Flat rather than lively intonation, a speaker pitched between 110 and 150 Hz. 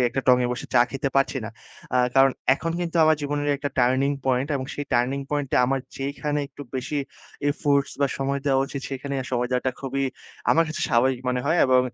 Yes: narrow, 1.9 semitones; low, 135 Hz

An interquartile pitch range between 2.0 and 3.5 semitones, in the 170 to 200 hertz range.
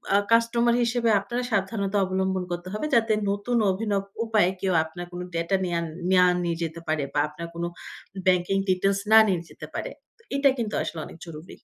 No: average, 4.1 semitones; high, 190 Hz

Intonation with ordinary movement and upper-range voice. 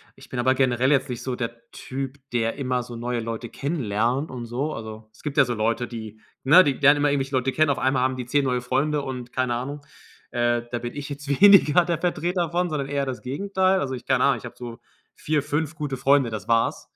No: average, 3.1 semitones; low, 130 Hz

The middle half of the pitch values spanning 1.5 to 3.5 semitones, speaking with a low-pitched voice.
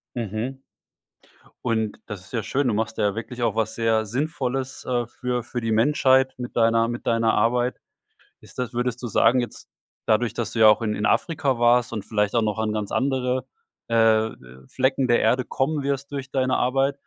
Yes: average, 2.7 semitones; low, 120 Hz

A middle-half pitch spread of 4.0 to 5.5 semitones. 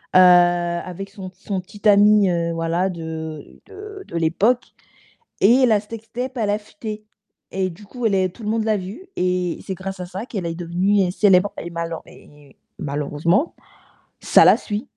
No: average, 3.6 semitones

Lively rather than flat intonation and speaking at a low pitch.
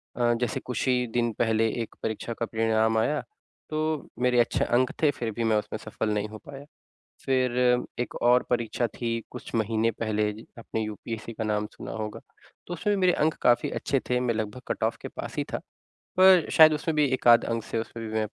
No: narrow, 2.5 semitones; low, 115 Hz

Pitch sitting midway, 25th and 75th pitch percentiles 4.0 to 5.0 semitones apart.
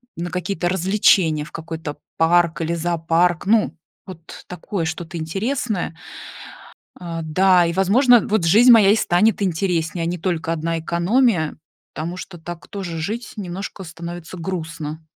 No: medium, 175 Hz; average, 2.8 semitones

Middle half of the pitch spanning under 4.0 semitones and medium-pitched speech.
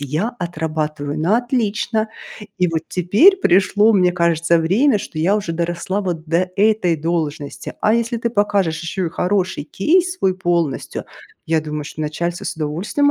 No: average, 4.4 semitones; medium, 175 Hz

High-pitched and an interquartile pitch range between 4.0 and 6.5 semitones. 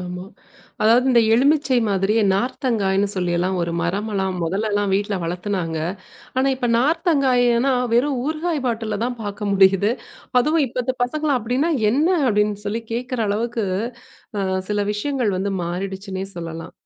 Yes: high, 215 Hz; average, 4.6 semitones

